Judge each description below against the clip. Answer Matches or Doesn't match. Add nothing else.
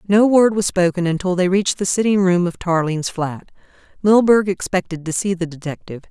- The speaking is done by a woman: Matches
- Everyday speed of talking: Matches